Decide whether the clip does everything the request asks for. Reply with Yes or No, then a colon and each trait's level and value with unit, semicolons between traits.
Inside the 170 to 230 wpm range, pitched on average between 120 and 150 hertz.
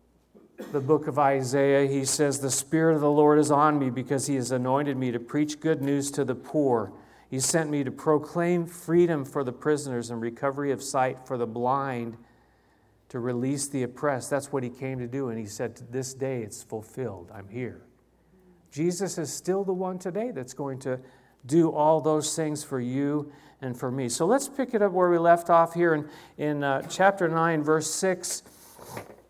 Yes: average, 200 wpm; medium, 140 Hz